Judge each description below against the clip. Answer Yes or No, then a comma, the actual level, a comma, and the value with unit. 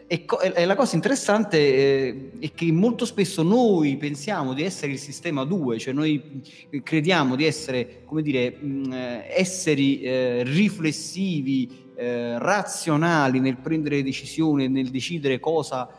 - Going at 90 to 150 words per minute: Yes, average, 120 wpm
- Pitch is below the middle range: No, medium, 145 Hz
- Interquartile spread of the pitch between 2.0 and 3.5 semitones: No, average, 4.0 semitones